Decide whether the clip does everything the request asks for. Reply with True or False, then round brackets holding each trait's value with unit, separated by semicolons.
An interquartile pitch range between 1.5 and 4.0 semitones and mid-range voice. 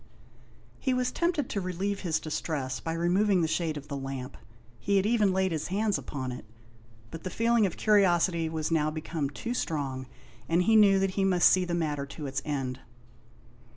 False (4.8 semitones; 170 Hz)